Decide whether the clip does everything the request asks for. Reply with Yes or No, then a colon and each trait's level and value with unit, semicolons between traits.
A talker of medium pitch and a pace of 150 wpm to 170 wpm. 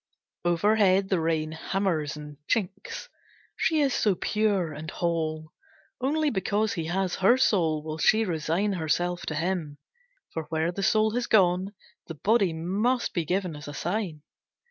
Yes: medium, 180 Hz; average, 155 wpm